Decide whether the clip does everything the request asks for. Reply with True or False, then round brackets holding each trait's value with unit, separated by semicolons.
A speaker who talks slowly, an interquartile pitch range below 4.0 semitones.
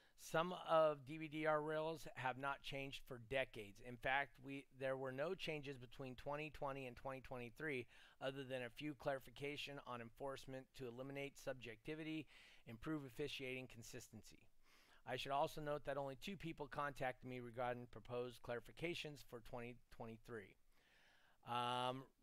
True (130 wpm; 3.0 semitones)